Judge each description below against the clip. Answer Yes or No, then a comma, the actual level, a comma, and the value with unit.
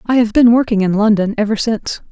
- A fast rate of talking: Yes, fast, 225 wpm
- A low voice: No, high, 220 Hz